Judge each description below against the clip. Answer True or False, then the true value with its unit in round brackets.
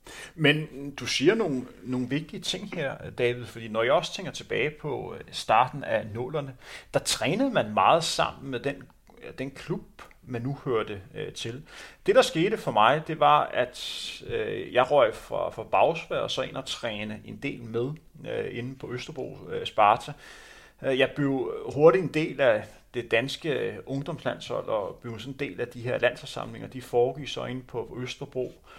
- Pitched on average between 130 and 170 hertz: True (135 Hz)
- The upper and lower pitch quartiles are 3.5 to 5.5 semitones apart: True (4.5 semitones)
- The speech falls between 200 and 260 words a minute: False (185 wpm)